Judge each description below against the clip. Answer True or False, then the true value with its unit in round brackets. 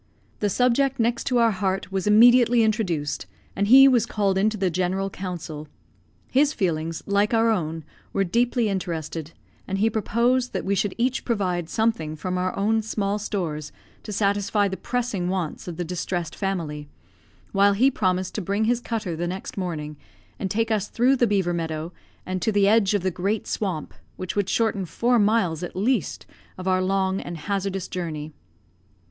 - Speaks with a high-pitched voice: True (195 Hz)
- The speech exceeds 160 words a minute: True (175 wpm)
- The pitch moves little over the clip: False (3.8 semitones)